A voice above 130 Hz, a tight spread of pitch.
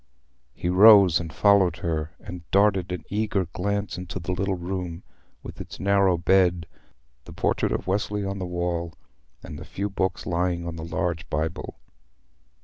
No: very low, 90 Hz; narrow, 2.3 semitones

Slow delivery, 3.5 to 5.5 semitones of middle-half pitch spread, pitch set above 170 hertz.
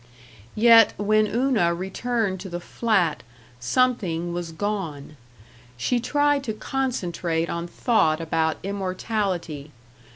Yes: slow, 105 wpm; average, 5.2 semitones; high, 190 Hz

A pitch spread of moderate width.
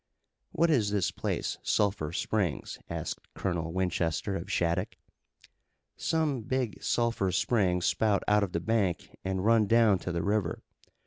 Yes: average, 4.1 semitones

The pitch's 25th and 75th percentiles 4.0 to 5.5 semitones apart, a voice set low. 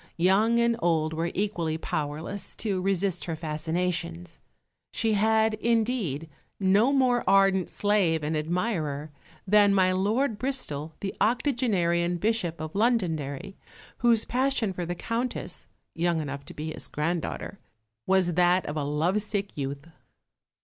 No: average, 5.2 semitones; medium, 185 Hz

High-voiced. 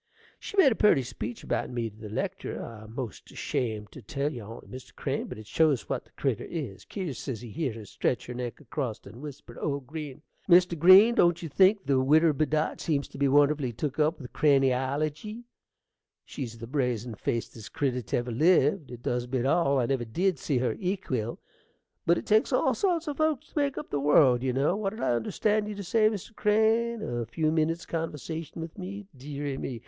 No: medium, 145 Hz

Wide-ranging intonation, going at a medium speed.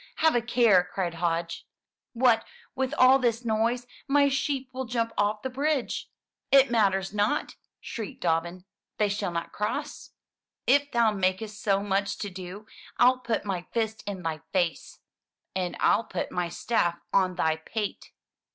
No: average, 4.7 semitones; average, 155 wpm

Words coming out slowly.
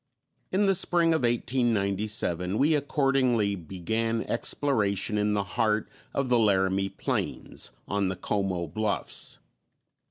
Yes: slow, 120 wpm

